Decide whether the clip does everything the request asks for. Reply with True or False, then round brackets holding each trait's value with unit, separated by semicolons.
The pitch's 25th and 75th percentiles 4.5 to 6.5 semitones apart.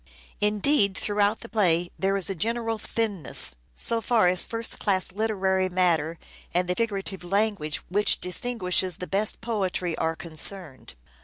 False (3.3 semitones)